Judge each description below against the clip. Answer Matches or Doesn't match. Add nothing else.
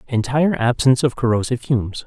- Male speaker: Matches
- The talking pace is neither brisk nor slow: Matches